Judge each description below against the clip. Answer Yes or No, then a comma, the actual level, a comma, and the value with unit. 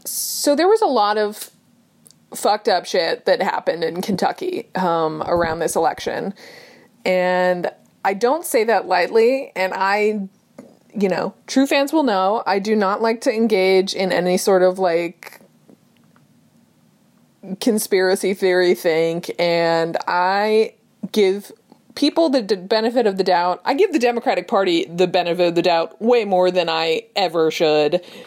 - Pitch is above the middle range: Yes, high, 195 Hz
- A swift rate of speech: No, average, 150 wpm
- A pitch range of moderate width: Yes, average, 4.9 semitones